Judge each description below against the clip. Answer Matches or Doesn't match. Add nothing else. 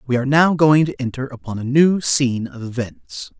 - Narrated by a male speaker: Matches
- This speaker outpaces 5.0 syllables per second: Matches